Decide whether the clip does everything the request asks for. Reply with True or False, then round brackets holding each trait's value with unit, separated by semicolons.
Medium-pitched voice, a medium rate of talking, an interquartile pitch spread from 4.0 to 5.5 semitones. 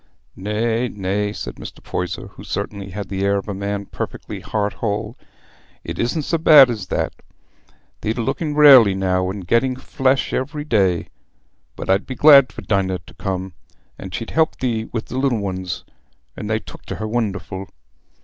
False (105 Hz; 170 wpm; 4.5 semitones)